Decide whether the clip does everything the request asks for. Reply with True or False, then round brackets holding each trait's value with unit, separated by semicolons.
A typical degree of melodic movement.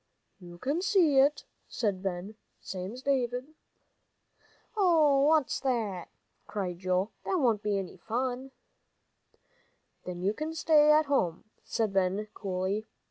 False (7.1 semitones)